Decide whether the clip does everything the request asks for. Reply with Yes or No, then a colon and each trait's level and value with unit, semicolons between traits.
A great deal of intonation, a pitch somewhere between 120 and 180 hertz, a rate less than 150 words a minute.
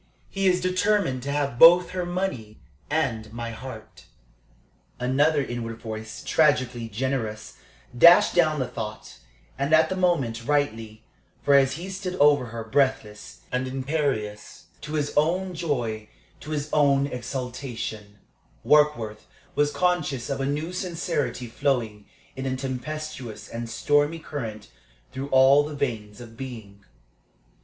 No: average, 5.0 semitones; low, 135 Hz; slow, 135 wpm